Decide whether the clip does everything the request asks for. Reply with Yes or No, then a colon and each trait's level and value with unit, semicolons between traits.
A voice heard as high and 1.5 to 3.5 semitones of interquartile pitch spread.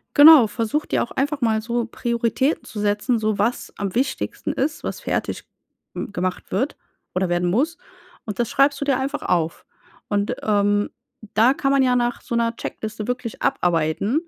No: high, 230 Hz; average, 4.5 semitones